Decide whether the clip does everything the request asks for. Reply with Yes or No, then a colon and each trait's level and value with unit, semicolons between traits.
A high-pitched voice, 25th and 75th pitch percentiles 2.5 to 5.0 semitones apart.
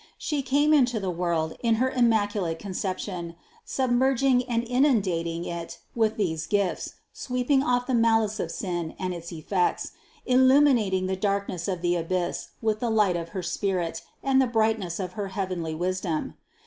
No: high, 200 Hz; wide, 5.5 semitones